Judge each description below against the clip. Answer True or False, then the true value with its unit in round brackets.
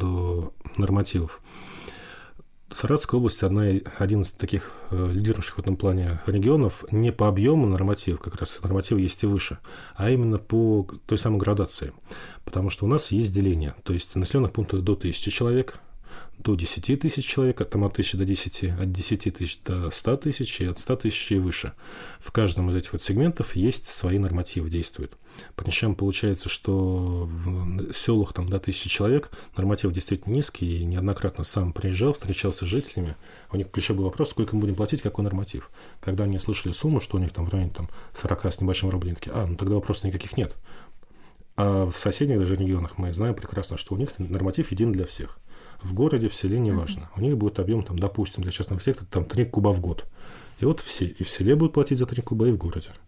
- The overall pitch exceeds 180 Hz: False (100 Hz)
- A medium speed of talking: False (195 wpm)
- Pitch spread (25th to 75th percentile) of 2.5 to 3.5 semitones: True (2.9 semitones)